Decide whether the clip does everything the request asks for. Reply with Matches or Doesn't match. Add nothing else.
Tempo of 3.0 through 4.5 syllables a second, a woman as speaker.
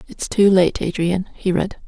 Matches